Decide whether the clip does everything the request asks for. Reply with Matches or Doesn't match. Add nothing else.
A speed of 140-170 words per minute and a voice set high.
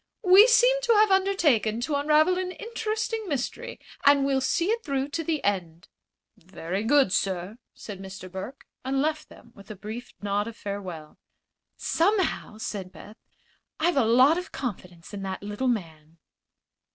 Matches